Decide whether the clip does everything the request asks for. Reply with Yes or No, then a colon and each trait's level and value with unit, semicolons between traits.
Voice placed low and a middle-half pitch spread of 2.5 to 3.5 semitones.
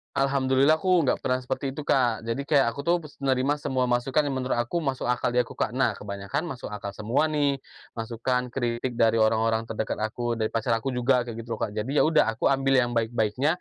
Yes: low, 125 Hz; average, 3.1 semitones